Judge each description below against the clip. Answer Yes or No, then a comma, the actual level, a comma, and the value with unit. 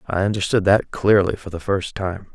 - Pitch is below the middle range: Yes, very low, 95 Hz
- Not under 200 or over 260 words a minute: Yes, fast, 205 wpm